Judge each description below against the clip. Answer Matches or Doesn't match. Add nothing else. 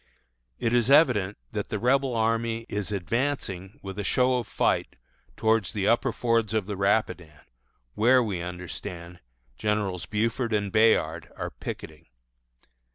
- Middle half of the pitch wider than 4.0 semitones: Doesn't match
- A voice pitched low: Matches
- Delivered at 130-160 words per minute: Matches